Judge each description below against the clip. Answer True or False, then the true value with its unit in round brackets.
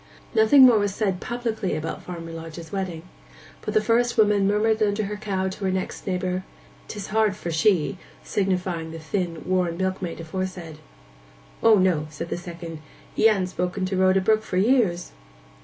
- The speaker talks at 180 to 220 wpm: False (170 wpm)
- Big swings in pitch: False (3.3 semitones)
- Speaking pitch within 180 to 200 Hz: True (190 Hz)